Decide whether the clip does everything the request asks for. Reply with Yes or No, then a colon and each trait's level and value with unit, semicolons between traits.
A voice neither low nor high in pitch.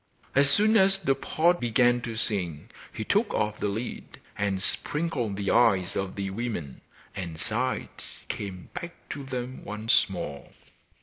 No: low, 115 Hz